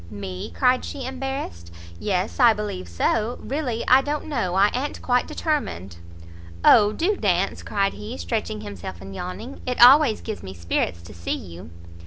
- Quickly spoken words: No, average, 165 wpm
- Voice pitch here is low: No, high, 210 Hz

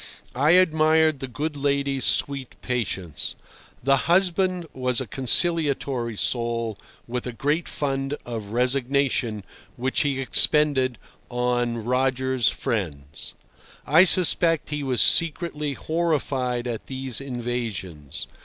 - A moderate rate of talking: No, slow, 110 wpm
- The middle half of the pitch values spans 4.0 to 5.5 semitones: No, average, 3.5 semitones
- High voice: No, low, 130 Hz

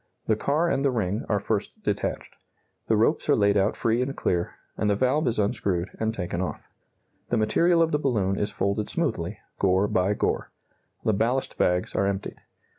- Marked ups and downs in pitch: No, average, 4.3 semitones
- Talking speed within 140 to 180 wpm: No, average, 190 wpm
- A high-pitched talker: No, low, 105 Hz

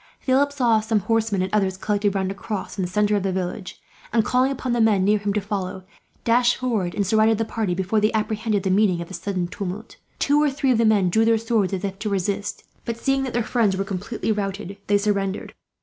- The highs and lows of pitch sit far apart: No, average, 2.8 semitones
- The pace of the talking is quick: Yes, fast, 240 wpm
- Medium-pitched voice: No, high, 210 Hz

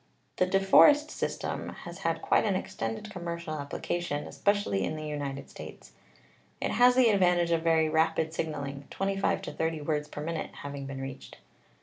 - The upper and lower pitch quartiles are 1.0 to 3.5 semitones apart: No, average, 4.3 semitones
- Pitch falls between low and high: Yes, medium, 160 Hz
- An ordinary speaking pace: Yes, average, 175 wpm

